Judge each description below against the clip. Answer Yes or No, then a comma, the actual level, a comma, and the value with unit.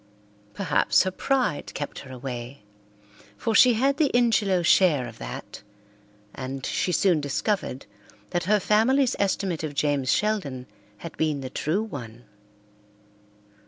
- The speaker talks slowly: Yes, slow, 130 wpm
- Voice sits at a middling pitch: Yes, medium, 165 Hz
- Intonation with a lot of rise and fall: Yes, wide, 7.7 semitones